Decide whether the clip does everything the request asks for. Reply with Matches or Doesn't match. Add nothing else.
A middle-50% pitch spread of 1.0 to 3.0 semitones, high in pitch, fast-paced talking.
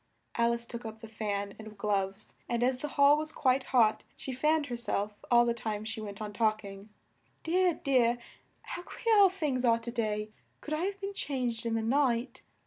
Doesn't match